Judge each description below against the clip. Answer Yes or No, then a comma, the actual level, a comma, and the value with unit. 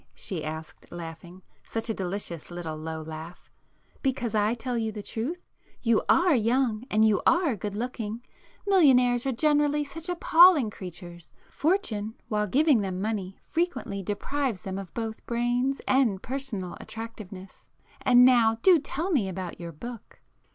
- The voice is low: No, high, 225 Hz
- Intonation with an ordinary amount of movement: No, wide, 5.8 semitones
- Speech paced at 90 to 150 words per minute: Yes, average, 145 wpm